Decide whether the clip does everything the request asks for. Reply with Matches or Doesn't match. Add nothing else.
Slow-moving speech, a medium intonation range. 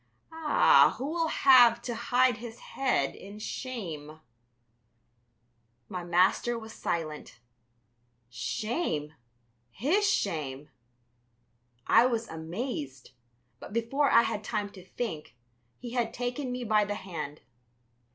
Doesn't match